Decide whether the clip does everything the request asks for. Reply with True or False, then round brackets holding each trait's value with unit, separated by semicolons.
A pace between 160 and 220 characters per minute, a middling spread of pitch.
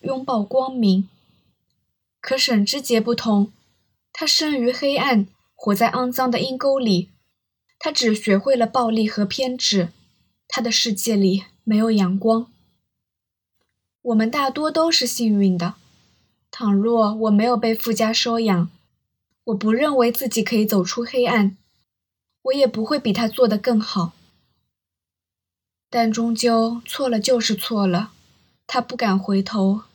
True (195 characters per minute; 4.1 semitones)